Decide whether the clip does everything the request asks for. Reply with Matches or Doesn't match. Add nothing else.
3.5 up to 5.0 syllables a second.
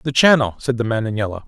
Doesn't match